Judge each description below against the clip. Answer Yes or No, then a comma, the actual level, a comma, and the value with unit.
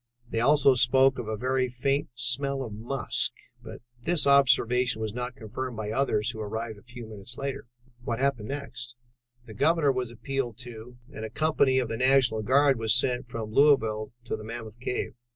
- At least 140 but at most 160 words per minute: No, average, 180 wpm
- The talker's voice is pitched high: No, low, 125 Hz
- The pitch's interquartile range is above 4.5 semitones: No, average, 3.4 semitones